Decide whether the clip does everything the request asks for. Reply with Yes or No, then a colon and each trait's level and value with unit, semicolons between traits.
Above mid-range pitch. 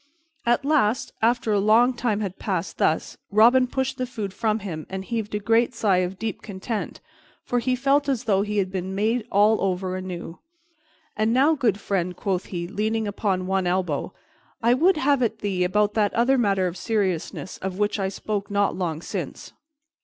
Yes: high, 210 Hz